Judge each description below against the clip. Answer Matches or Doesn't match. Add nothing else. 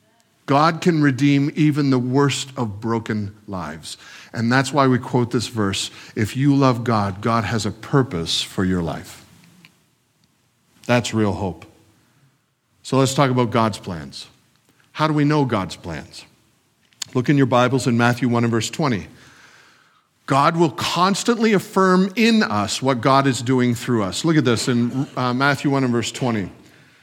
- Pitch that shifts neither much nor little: Matches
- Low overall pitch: Matches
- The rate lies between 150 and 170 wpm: Matches